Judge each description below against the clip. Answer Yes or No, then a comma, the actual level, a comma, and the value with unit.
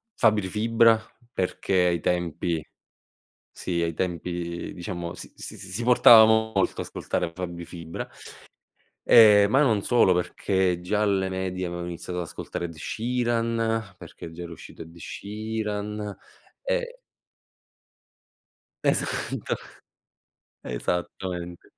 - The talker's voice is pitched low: Yes, very low, 95 Hz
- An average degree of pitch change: Yes, average, 4.2 semitones